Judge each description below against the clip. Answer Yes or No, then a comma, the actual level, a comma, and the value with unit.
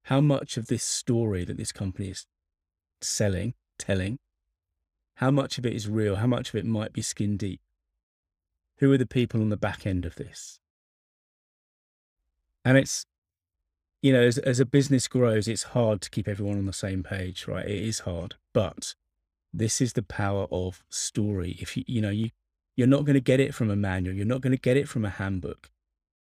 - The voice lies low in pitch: Yes, low, 100 Hz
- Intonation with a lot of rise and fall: Yes, wide, 6.2 semitones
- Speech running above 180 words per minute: Yes, average, 200 wpm